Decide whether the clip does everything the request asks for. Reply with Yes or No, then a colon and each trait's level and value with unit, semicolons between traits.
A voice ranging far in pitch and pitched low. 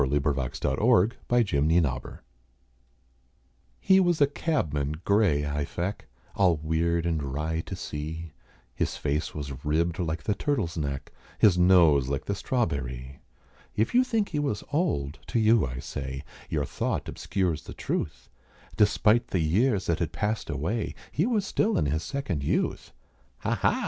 Yes: wide, 7.0 semitones; very low, 85 Hz